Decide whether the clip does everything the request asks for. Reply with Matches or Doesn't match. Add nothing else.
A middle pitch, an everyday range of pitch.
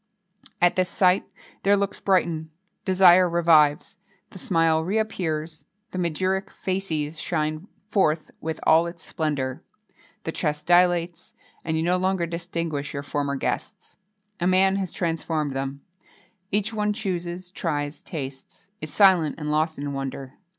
Matches